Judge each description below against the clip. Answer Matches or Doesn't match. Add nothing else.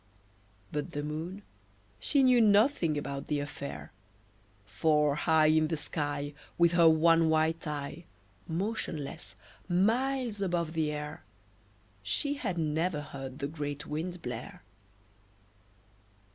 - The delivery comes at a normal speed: Doesn't match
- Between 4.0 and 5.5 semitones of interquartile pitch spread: Doesn't match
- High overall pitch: Doesn't match